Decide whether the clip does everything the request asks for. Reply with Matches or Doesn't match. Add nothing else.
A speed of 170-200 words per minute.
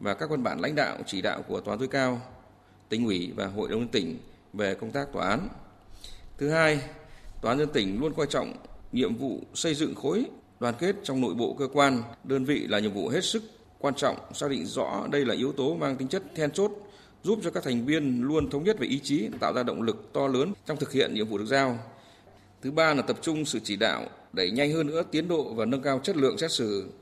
Doesn't match